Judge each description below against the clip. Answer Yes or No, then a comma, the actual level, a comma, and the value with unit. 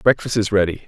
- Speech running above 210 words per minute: No, fast, 205 wpm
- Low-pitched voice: Yes, low, 105 Hz